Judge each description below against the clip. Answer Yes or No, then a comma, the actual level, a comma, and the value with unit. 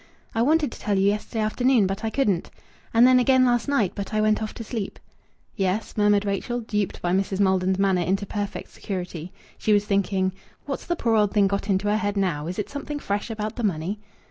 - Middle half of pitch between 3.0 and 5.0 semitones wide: No, narrow, 2.6 semitones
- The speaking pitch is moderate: No, high, 205 Hz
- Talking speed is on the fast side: Yes, fast, 220 wpm